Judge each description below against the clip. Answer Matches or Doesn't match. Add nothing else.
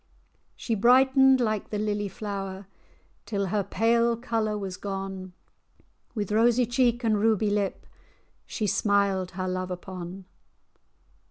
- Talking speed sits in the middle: Doesn't match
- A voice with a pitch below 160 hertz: Doesn't match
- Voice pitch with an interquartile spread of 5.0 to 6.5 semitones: Doesn't match